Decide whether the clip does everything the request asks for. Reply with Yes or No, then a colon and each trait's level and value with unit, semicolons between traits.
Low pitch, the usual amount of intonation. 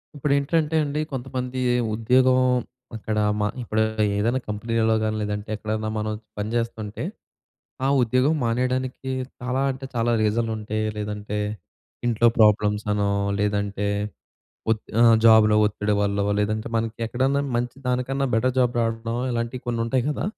Yes: low, 115 Hz; average, 3.1 semitones